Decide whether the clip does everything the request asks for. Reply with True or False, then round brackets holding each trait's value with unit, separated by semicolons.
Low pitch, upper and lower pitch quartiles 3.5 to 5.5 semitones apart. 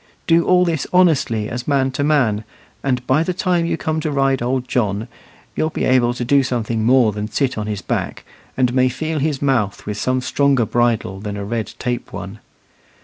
True (130 Hz; 4.2 semitones)